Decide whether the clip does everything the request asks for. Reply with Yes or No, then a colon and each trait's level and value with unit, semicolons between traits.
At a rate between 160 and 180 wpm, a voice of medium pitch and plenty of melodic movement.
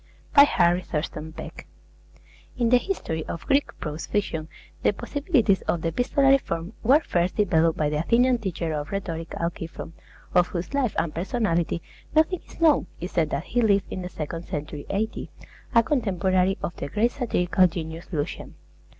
Yes: average, 165 wpm; medium, 180 Hz; wide, 6.2 semitones